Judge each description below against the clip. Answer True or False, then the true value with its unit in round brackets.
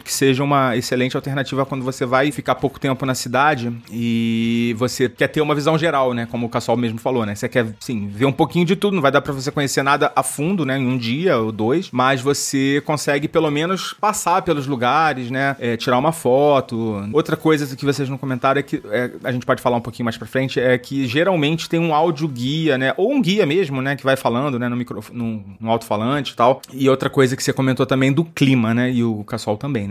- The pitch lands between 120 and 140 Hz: True (135 Hz)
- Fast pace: True (240 wpm)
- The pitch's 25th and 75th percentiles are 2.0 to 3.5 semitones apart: True (2.9 semitones)